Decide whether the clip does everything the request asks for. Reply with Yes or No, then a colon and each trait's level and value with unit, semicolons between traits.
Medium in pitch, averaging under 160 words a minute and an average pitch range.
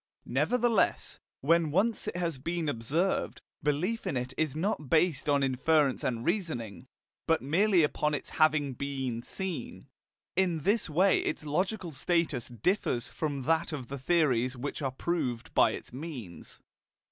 Yes: medium, 155 Hz; average, 145 wpm; average, 4.7 semitones